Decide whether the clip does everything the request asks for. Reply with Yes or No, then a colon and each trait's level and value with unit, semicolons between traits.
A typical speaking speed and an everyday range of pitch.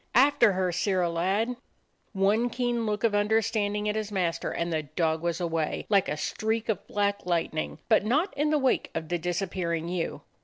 Yes: average, 190 wpm; average, 4.4 semitones